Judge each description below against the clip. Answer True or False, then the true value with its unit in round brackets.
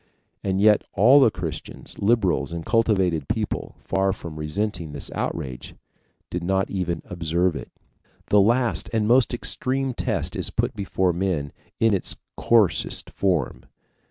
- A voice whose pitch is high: False (95 Hz)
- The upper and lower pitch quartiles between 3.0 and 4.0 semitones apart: False (4.5 semitones)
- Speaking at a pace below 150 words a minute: True (140 wpm)